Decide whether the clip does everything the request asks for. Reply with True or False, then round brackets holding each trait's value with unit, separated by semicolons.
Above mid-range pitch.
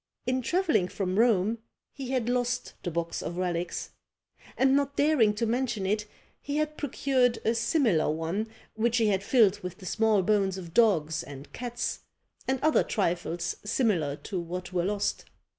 True (215 Hz)